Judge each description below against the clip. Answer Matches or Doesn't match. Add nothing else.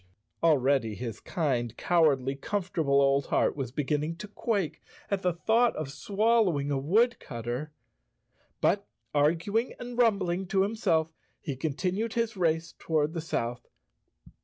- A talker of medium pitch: Matches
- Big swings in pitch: Matches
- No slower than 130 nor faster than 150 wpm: Matches